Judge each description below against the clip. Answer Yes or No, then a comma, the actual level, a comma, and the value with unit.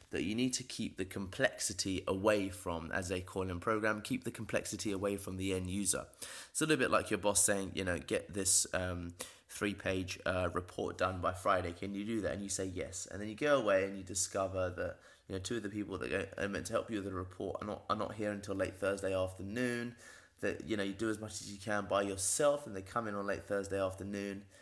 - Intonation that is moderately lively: No, narrow, 2.2 semitones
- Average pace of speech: No, fast, 250 wpm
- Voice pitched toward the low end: Yes, low, 100 Hz